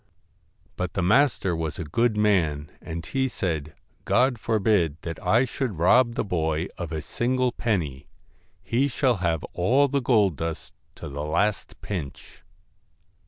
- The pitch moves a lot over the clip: Yes, wide, 6.7 semitones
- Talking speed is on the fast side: No, average, 155 wpm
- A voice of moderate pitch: No, very low, 95 Hz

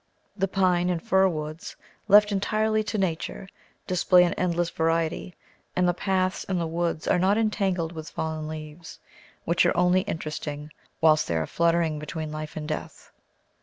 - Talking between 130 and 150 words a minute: No, average, 165 wpm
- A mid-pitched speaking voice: Yes, medium, 170 Hz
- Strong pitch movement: No, average, 3.0 semitones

